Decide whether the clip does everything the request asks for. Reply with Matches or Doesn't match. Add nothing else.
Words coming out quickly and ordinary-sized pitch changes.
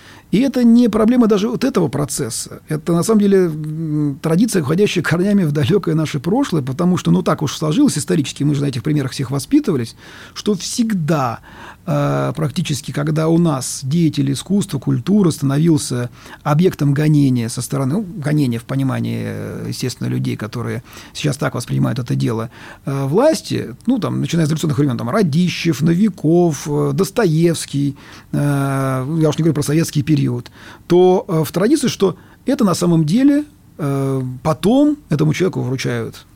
Doesn't match